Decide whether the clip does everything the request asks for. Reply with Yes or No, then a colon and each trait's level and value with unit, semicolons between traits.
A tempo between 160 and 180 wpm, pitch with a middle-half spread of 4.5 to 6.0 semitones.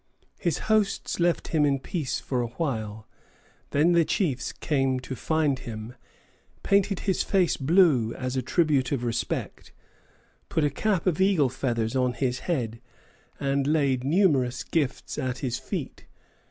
No: average, 150 wpm; average, 4.9 semitones